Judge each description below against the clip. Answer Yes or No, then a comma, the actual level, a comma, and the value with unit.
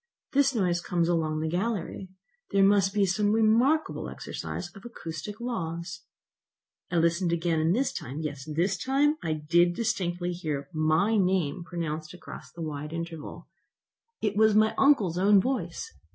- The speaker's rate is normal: Yes, average, 155 wpm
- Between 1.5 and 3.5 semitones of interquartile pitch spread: No, average, 4.3 semitones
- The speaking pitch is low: No, medium, 175 Hz